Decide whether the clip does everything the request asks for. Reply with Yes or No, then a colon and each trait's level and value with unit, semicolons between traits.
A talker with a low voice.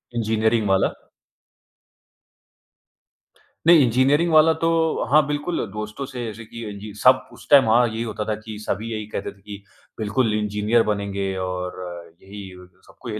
Yes: low, 110 Hz